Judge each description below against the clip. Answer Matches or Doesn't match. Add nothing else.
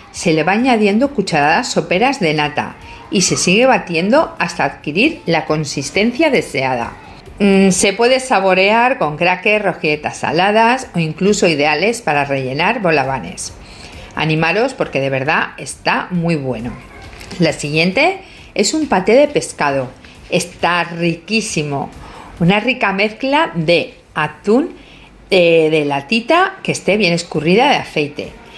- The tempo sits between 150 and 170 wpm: Doesn't match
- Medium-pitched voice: Matches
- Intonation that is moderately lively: Doesn't match